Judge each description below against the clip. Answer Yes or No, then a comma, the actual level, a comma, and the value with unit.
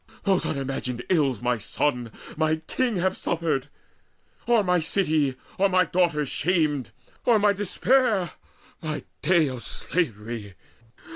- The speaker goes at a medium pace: No, slow, 120 wpm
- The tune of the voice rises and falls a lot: Yes, wide, 6.0 semitones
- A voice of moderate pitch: Yes, medium, 155 Hz